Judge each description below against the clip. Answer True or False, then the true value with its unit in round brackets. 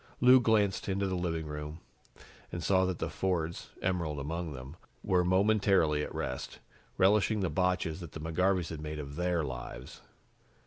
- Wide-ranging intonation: False (3.8 semitones)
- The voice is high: False (85 Hz)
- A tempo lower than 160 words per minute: False (165 wpm)